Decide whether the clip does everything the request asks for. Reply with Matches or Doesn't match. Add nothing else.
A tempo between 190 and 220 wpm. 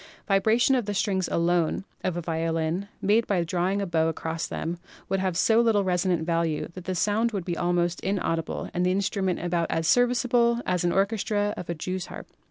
Matches